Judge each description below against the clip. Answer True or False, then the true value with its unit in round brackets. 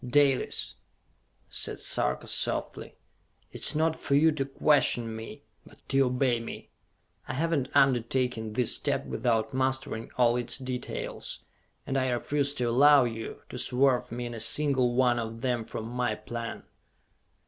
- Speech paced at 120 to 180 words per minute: True (155 wpm)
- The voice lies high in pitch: False (125 Hz)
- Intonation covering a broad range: False (2.6 semitones)